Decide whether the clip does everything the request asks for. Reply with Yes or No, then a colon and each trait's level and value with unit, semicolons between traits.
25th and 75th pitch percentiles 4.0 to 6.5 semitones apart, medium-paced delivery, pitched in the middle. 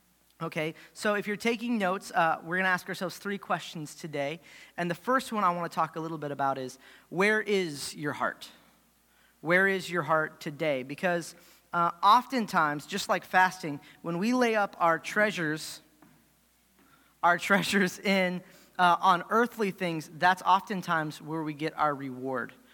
No: average, 3.6 semitones; average, 165 wpm; medium, 175 Hz